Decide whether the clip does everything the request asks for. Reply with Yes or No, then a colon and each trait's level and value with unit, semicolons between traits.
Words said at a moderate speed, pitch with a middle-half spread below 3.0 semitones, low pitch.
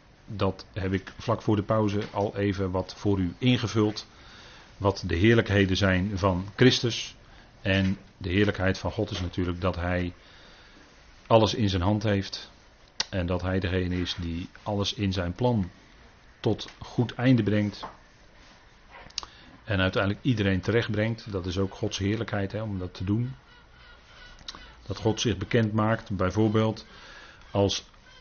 Yes: average, 145 wpm; narrow, 2.5 semitones; low, 100 Hz